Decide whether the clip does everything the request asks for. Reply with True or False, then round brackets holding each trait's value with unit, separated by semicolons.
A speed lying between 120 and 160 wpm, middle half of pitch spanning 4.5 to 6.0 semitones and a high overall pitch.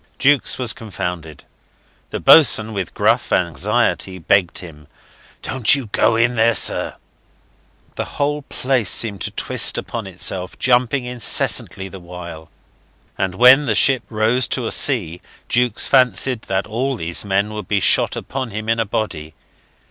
False (150 wpm; 4.9 semitones; 110 Hz)